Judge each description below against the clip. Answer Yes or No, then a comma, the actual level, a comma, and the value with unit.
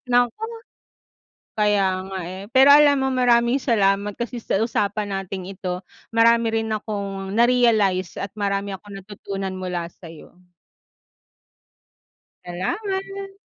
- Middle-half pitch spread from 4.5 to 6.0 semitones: No, average, 3.8 semitones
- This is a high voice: Yes, high, 205 Hz